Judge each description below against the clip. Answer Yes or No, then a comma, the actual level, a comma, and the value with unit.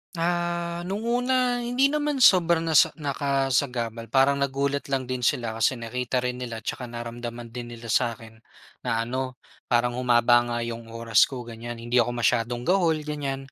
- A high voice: No, low, 125 Hz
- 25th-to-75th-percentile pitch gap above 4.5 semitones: Yes, average, 5.2 semitones